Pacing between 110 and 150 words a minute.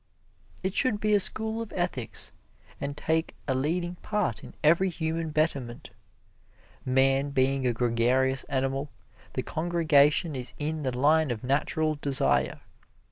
Yes: slow, 135 wpm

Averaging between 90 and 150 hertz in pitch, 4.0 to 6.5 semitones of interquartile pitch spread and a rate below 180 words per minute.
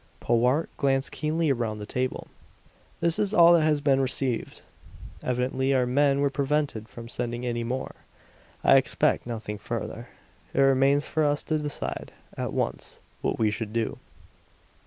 No: low, 135 Hz; average, 3.5 semitones; average, 155 wpm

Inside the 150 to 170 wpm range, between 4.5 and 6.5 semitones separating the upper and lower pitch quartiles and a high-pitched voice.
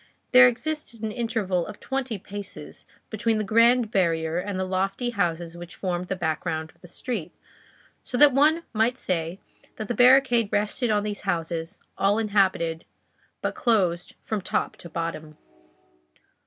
Yes: average, 155 wpm; average, 5.1 semitones; high, 205 Hz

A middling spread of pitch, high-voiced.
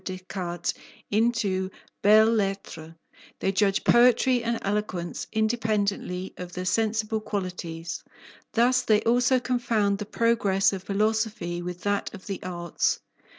Yes: average, 3.4 semitones; high, 205 Hz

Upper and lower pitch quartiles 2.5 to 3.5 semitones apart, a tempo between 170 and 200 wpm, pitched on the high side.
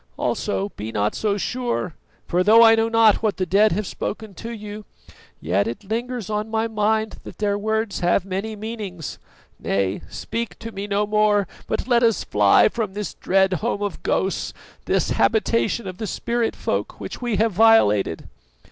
Yes: average, 2.8 semitones; average, 175 wpm; high, 210 Hz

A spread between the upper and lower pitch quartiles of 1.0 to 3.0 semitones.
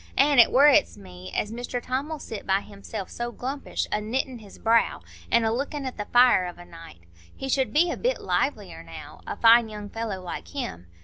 No: average, 5.1 semitones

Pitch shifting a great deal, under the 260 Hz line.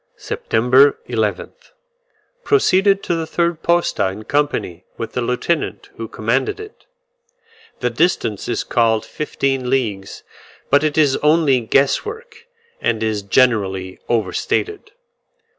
Yes: wide, 7.1 semitones; low, 135 Hz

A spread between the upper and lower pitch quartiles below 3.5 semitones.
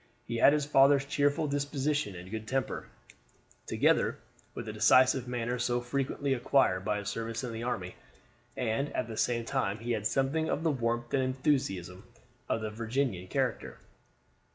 No: average, 3.8 semitones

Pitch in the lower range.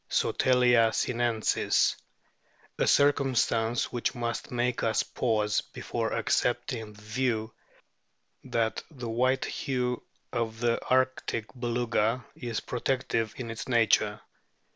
Yes: low, 120 Hz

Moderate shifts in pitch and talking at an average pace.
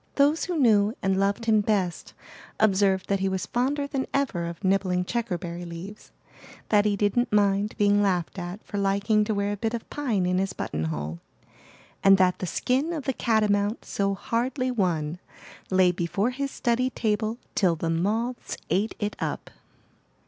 Yes: average, 3.8 semitones; average, 170 wpm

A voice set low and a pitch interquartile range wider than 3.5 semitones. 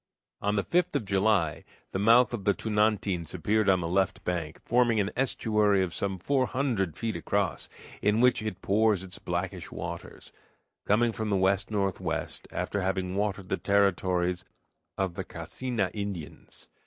No: low, 100 Hz; narrow, 2.6 semitones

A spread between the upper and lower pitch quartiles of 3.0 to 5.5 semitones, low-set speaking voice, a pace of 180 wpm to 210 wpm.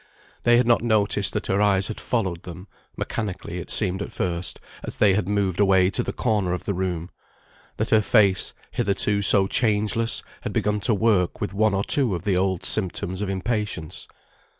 No: narrow, 2.5 semitones; low, 100 Hz; average, 190 wpm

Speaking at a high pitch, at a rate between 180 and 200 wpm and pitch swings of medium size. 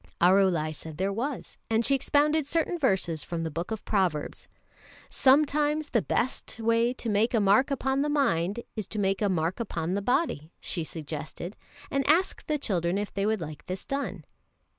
No: high, 210 Hz; average, 185 wpm; wide, 7.7 semitones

